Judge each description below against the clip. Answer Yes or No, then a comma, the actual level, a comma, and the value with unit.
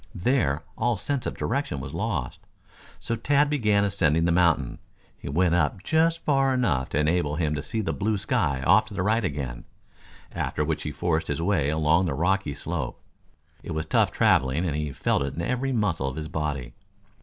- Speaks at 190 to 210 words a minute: Yes, average, 195 wpm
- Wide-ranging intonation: Yes, wide, 6.5 semitones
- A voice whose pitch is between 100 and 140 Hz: No, very low, 85 Hz